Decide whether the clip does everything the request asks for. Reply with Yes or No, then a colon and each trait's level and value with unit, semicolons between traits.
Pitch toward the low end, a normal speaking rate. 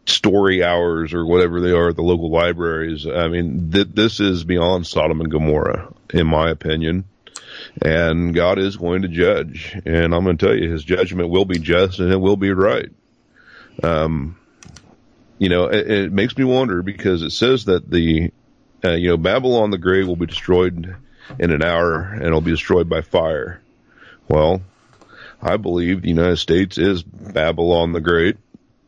Yes: very low, 85 Hz; average, 175 wpm